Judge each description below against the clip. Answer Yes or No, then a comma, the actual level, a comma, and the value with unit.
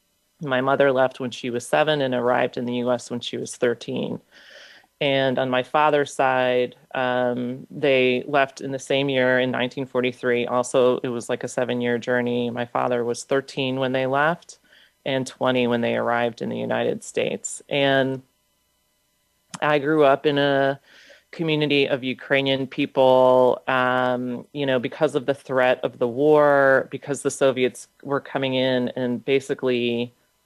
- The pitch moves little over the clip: Yes, narrow, 1.8 semitones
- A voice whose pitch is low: Yes, low, 130 Hz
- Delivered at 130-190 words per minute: Yes, average, 160 wpm